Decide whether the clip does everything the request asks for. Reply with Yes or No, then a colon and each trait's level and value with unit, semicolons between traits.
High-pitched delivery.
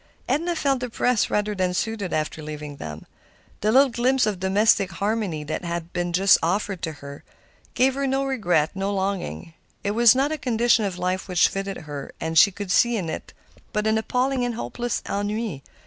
Yes: high, 205 Hz